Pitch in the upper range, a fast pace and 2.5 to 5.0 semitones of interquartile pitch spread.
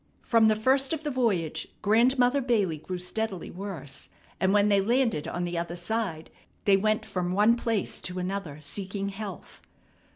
No: high, 200 Hz; average, 165 wpm; average, 4.2 semitones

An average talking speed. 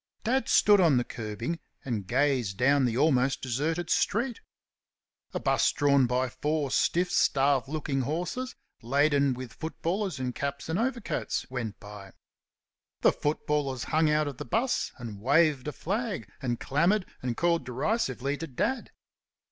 Yes: average, 150 wpm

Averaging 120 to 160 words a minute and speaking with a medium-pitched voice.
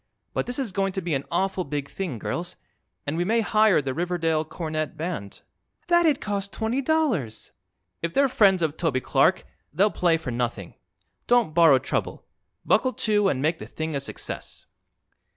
No: average, 170 wpm; medium, 175 Hz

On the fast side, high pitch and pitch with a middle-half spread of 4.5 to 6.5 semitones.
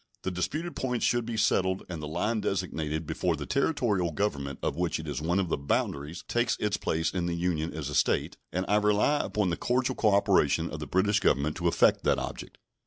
No: fast, 215 wpm; very low, 90 Hz; average, 4.9 semitones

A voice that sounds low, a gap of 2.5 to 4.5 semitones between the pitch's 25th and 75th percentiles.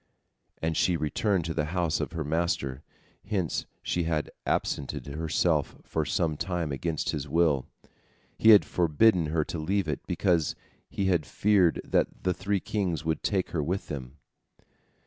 Yes: very low, 85 Hz; average, 3.2 semitones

